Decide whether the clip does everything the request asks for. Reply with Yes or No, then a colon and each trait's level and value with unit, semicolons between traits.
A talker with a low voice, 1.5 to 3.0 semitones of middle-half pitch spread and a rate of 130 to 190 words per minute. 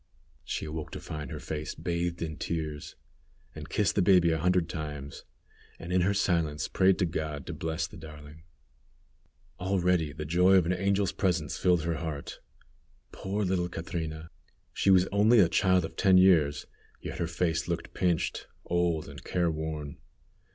Yes: very low, 85 Hz; average, 2.7 semitones; average, 160 wpm